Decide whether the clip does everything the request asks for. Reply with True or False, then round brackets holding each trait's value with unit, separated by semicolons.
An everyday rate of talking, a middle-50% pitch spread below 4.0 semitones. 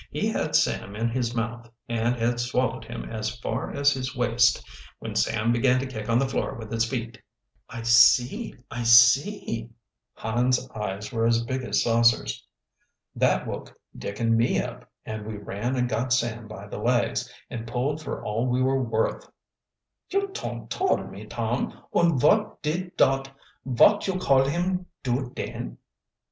True (170 wpm; 2.5 semitones)